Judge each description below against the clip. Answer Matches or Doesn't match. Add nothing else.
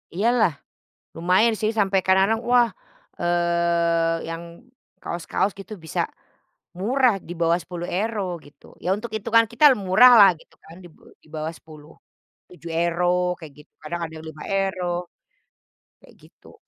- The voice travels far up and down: Doesn't match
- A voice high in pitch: Doesn't match